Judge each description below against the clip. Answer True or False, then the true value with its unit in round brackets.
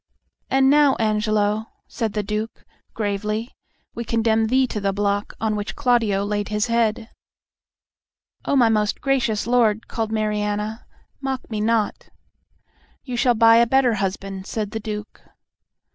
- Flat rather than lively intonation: True (2.1 semitones)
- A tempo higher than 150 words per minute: False (145 wpm)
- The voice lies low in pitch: False (220 Hz)